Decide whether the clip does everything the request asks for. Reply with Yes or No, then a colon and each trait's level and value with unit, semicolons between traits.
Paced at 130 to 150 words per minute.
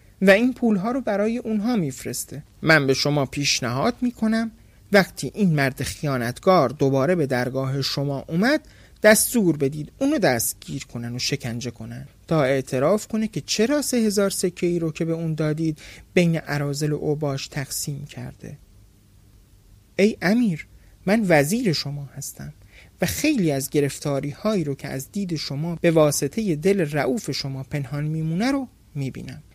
Yes: average, 145 wpm